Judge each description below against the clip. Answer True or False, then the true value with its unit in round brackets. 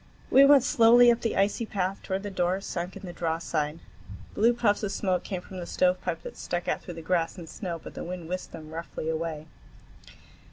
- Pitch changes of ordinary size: True (3.5 semitones)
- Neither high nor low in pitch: True (180 Hz)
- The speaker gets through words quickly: True (210 wpm)